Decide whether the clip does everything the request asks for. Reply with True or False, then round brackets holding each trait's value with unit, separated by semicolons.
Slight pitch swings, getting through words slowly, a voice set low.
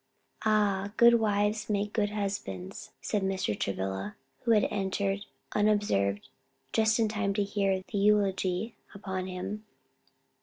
False (2.0 semitones; 125 wpm; 200 Hz)